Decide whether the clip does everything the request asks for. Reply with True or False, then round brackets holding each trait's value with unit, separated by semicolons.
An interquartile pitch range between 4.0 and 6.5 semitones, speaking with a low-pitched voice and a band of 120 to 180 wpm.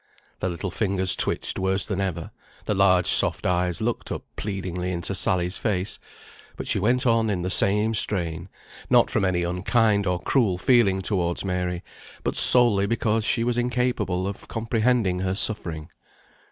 False (3.6 semitones; 95 Hz; 160 wpm)